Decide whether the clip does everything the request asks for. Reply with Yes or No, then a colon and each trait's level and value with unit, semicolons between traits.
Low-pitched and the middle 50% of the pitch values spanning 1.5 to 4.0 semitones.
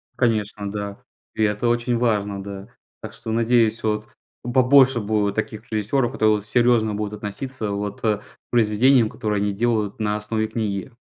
Yes: low, 110 Hz; narrow, 2.4 semitones